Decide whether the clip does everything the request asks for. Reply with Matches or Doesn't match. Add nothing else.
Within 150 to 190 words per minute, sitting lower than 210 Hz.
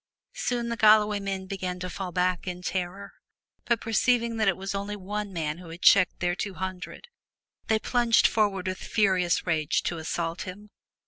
Matches